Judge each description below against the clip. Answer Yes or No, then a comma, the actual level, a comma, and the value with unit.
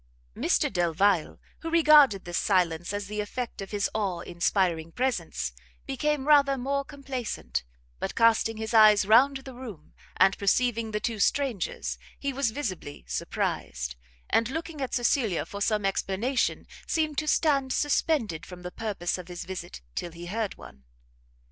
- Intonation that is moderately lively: No, wide, 6.6 semitones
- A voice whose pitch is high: Yes, high, 215 Hz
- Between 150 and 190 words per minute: Yes, average, 155 wpm